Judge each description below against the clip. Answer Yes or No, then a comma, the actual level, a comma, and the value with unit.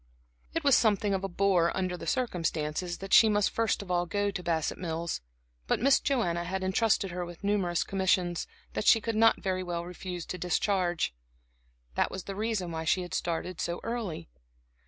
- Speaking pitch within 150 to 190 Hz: Yes, medium, 185 Hz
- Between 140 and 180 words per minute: No, average, 190 wpm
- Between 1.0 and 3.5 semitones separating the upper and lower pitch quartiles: Yes, average, 2.8 semitones